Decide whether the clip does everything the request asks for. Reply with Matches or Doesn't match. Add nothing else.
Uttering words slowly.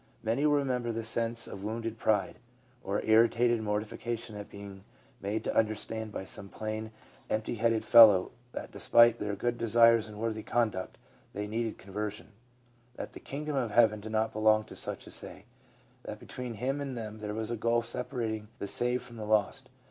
Doesn't match